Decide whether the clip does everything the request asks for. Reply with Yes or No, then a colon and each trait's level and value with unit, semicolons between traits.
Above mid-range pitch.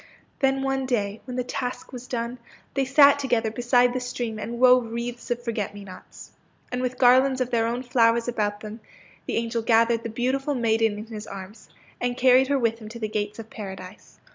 Yes: high, 235 Hz